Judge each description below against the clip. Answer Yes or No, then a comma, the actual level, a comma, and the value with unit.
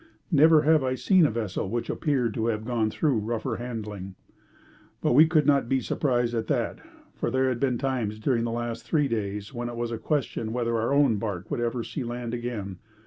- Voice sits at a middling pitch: No, low, 120 Hz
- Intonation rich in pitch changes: No, average, 3.1 semitones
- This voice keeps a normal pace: No, fast, 210 wpm